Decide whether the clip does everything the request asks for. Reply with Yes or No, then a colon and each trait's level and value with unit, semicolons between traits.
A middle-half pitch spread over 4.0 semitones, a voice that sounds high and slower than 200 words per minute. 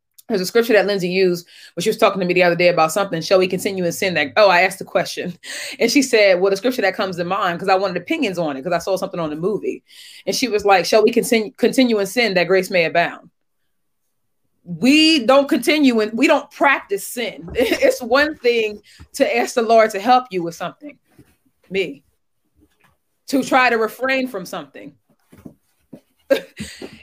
No: wide, 5.6 semitones; high, 210 Hz; fast, 205 wpm